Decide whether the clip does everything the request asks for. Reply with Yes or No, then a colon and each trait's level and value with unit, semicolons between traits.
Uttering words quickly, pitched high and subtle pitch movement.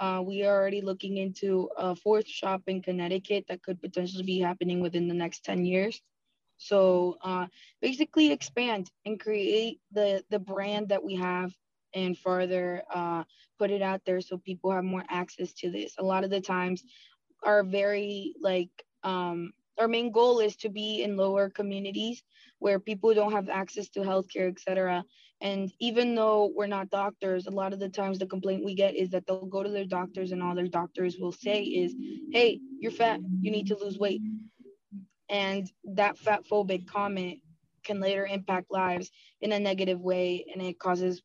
No: average, 185 wpm; high, 195 Hz; narrow, 2.1 semitones